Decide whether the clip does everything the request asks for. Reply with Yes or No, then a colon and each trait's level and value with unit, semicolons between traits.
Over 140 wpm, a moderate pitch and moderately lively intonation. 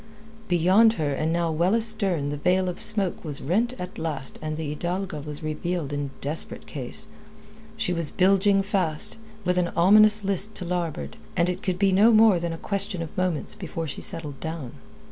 Yes: average, 185 wpm; medium, 175 Hz; average, 3.9 semitones